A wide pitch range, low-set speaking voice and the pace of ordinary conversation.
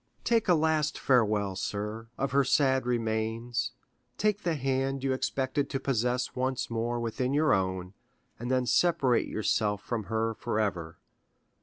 No: average, 3.7 semitones; low, 125 Hz; average, 145 wpm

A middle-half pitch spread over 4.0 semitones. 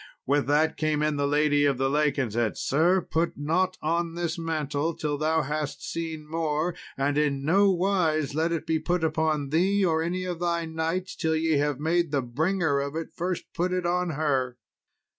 No: average, 2.7 semitones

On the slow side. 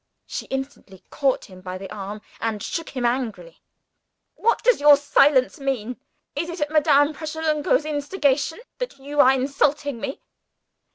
No: average, 150 wpm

